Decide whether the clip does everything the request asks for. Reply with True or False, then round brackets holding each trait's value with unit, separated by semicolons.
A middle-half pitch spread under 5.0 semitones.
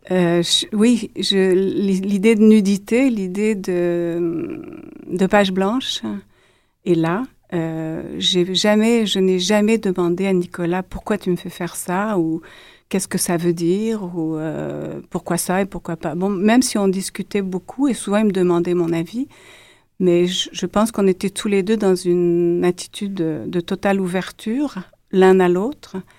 True (2.9 semitones)